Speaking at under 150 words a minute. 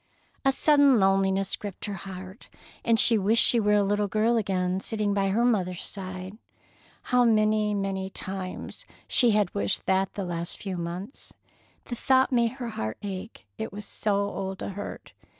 No: average, 170 wpm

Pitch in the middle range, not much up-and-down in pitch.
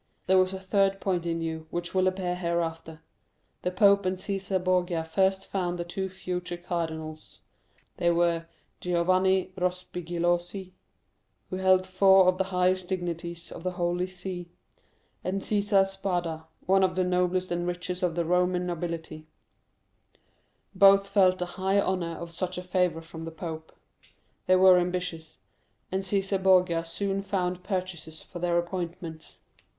Yes: medium, 180 Hz; narrow, 1.6 semitones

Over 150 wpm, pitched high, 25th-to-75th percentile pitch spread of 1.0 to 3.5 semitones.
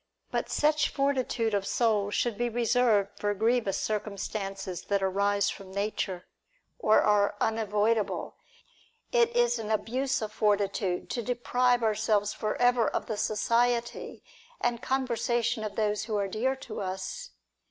No: average, 140 wpm; high, 220 Hz; average, 3.1 semitones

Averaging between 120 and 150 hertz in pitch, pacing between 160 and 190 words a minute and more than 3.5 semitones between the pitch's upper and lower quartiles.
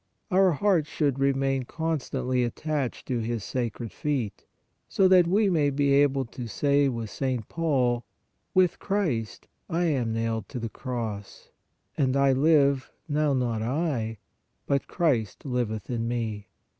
No: low, 135 Hz; average, 145 wpm; average, 4.3 semitones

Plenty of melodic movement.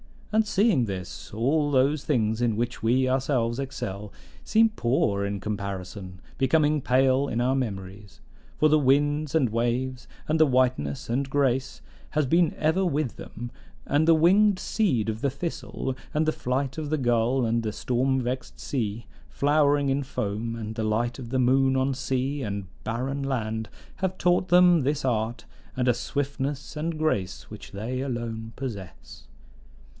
No: average, 4.3 semitones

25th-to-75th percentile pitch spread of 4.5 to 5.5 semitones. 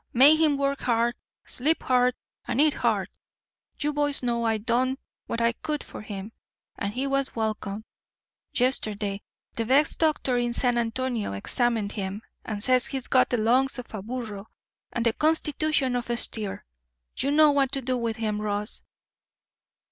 No: average, 3.6 semitones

